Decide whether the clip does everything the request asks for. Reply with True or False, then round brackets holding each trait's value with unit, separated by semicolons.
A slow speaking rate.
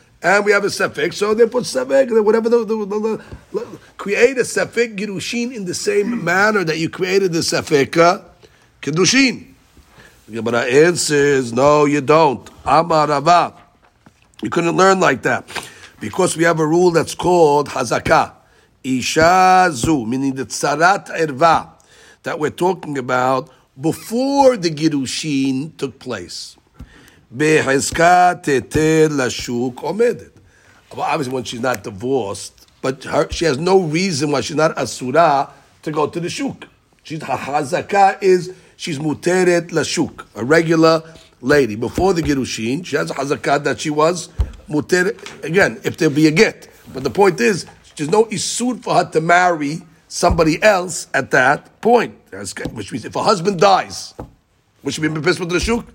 False (150 wpm)